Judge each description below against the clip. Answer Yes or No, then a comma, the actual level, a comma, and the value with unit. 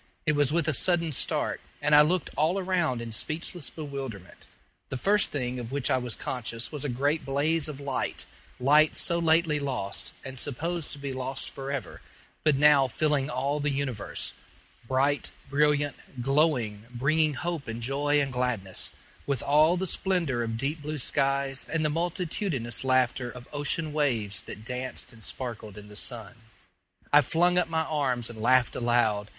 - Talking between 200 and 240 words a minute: No, average, 170 wpm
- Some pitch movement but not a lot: Yes, average, 3.8 semitones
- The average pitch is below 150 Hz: Yes, medium, 140 Hz